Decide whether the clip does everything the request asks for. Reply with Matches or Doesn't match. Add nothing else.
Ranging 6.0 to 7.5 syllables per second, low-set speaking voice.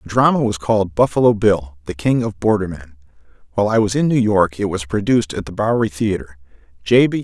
Matches